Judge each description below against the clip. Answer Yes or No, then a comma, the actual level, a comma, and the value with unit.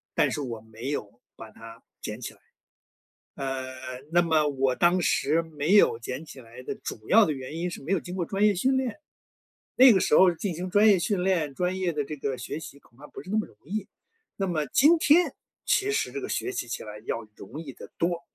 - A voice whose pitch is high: No, medium, 160 Hz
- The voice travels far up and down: Yes, wide, 6.6 semitones